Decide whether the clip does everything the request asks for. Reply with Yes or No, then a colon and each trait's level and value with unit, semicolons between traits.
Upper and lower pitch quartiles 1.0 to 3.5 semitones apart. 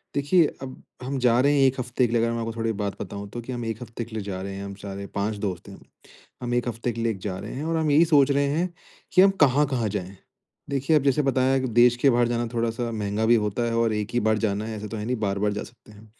No: average, 3.9 semitones